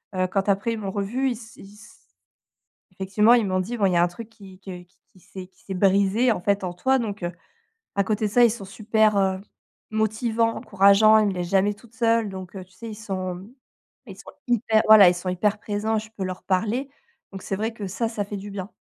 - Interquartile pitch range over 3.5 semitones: No, narrow, 2.6 semitones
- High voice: Yes, high, 205 Hz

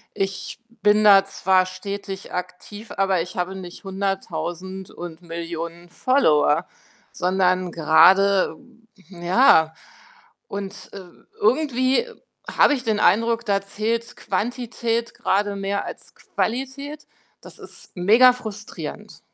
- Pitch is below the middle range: No, high, 195 Hz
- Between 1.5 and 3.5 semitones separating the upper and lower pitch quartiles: No, average, 3.9 semitones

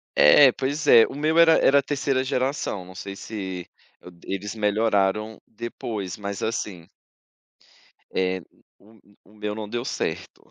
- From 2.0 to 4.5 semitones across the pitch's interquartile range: No, average, 4.9 semitones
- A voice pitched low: Yes, low, 105 Hz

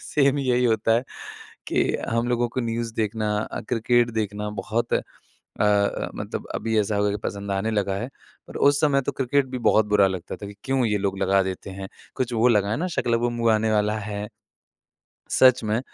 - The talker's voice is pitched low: Yes, low, 110 Hz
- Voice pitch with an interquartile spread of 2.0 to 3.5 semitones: Yes, average, 2.9 semitones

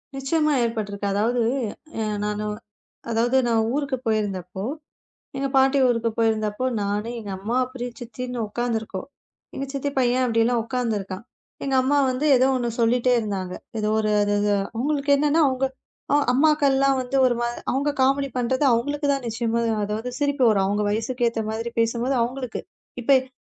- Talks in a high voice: Yes, high, 240 Hz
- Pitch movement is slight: No, average, 3.5 semitones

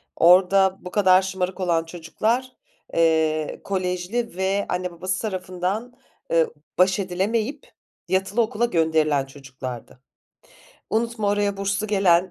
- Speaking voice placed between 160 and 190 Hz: Yes, medium, 185 Hz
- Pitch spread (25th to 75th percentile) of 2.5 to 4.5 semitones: Yes, average, 3.2 semitones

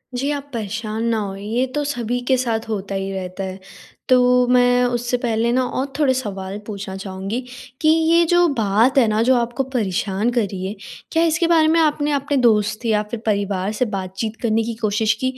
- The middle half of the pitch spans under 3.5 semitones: No, average, 4.2 semitones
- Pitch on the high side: Yes, high, 230 Hz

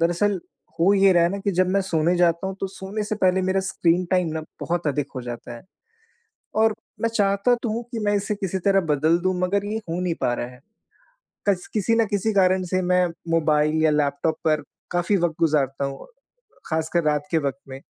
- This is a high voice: No, medium, 180 Hz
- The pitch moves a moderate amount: Yes, average, 3.9 semitones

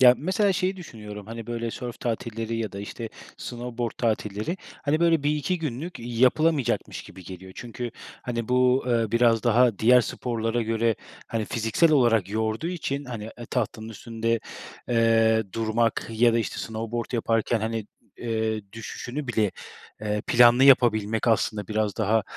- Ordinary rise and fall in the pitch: No, narrow, 2.0 semitones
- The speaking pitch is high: No, low, 115 Hz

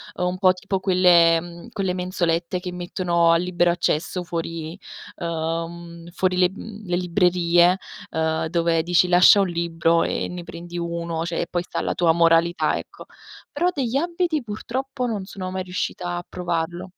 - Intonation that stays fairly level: Yes, narrow, 1.6 semitones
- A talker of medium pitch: Yes, medium, 175 Hz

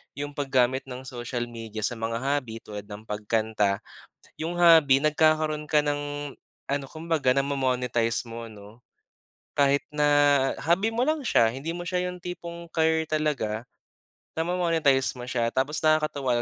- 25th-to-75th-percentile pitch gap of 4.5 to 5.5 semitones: Yes, average, 4.8 semitones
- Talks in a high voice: No, medium, 140 Hz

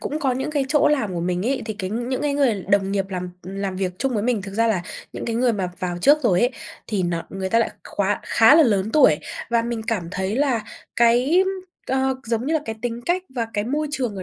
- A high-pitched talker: Yes, high, 230 Hz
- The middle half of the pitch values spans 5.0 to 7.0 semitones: Yes, wide, 5.4 semitones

